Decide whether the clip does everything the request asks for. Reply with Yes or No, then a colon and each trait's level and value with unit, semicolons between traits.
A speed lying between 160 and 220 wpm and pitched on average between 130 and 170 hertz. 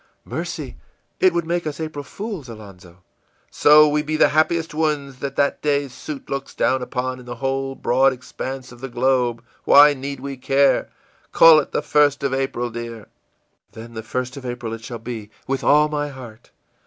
Yes: average, 190 wpm; low, 135 Hz